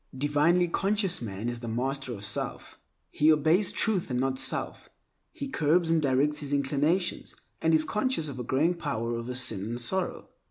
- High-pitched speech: No, medium, 145 Hz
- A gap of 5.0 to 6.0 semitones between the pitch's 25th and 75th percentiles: Yes, average, 5.3 semitones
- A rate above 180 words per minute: No, average, 175 wpm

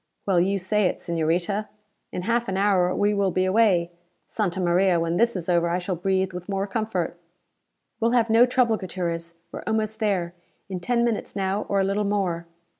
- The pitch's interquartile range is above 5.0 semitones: No, average, 3.1 semitones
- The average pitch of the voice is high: Yes, high, 195 Hz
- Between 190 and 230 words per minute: Yes, average, 195 wpm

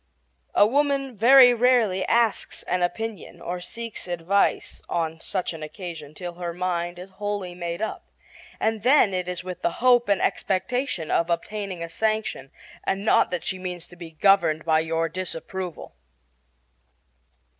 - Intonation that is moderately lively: Yes, average, 4.3 semitones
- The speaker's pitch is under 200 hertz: Yes, medium, 185 Hz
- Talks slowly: No, average, 155 wpm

